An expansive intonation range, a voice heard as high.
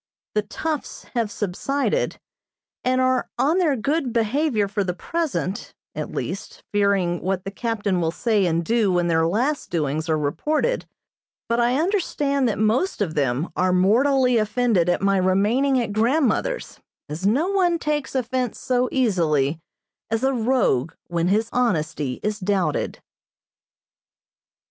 Yes: wide, 6.4 semitones; high, 220 Hz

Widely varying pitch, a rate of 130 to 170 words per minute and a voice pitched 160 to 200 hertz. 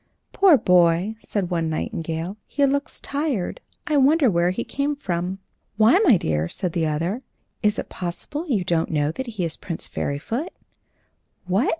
Yes: wide, 8.4 semitones; average, 165 wpm; high, 190 Hz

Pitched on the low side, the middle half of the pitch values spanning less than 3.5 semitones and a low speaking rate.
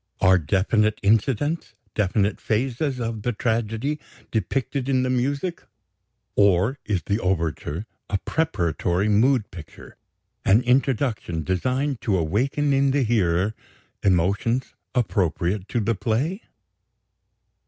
No: low, 110 Hz; average, 5.3 semitones; slow, 110 wpm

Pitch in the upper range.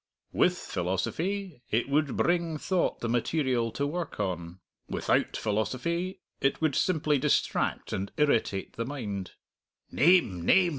No: medium, 140 Hz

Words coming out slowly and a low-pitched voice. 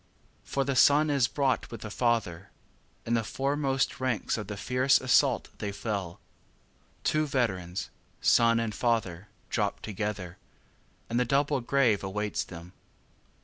No: average, 145 wpm; low, 115 Hz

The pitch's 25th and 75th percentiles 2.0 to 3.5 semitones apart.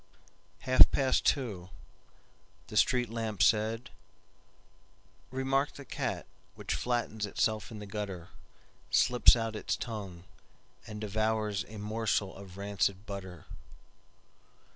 Yes: average, 2.7 semitones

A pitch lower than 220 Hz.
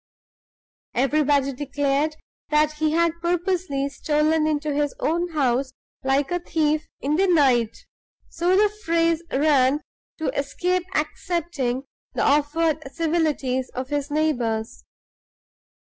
No: very high, 300 Hz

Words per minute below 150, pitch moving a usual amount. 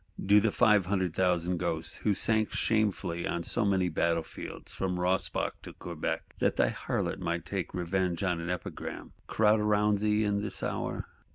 No: average, 170 wpm; average, 3.3 semitones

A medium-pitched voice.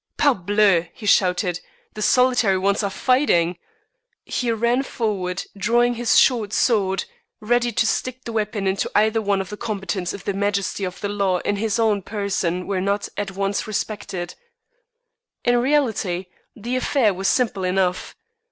No: high, 205 Hz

